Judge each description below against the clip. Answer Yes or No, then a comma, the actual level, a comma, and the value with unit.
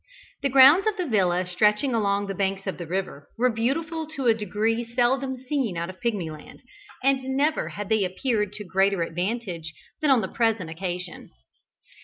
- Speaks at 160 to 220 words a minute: Yes, average, 175 wpm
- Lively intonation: Yes, wide, 5.8 semitones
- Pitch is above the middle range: Yes, high, 215 Hz